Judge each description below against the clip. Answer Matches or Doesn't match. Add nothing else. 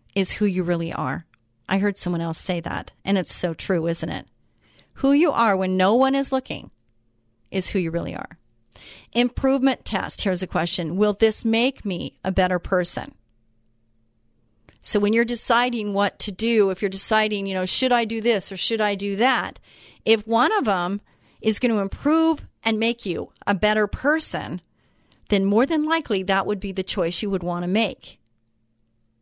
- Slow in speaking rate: Doesn't match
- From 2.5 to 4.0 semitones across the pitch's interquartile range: Doesn't match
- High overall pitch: Matches